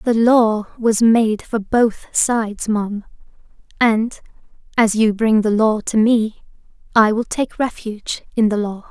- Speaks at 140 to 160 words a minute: Yes, average, 155 wpm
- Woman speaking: Yes, female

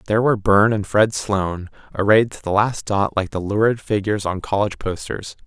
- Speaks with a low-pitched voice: Yes, low, 100 Hz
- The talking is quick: No, average, 195 wpm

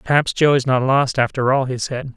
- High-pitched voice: No, low, 130 Hz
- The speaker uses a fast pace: Yes, fast, 250 wpm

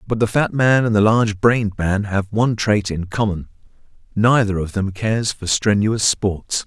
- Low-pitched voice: Yes, low, 105 Hz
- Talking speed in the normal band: Yes, average, 190 wpm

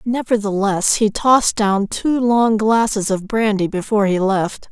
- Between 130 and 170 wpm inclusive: Yes, average, 155 wpm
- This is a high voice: Yes, high, 210 Hz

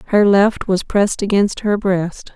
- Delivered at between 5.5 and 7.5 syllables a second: No, 4.3 syllables/s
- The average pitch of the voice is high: Yes, high, 200 Hz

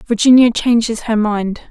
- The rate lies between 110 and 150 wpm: Yes, average, 140 wpm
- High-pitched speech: Yes, high, 225 Hz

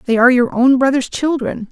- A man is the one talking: No, female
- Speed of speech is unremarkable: No, fast, 210 wpm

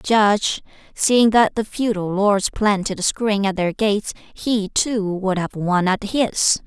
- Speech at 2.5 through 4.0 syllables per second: Yes, 3.9 syllables/s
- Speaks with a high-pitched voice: Yes, high, 205 Hz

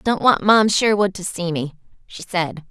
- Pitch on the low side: No, high, 190 Hz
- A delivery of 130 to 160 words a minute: No, average, 200 wpm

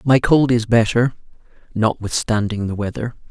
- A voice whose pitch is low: Yes, low, 115 Hz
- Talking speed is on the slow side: Yes, slow, 125 wpm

